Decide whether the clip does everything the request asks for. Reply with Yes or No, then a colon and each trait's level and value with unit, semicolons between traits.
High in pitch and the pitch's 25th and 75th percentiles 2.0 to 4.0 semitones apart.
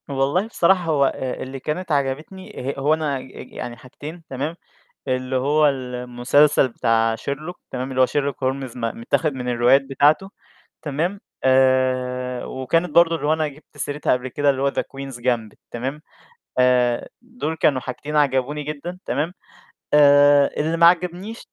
No: medium, 140 Hz; average, 3.2 semitones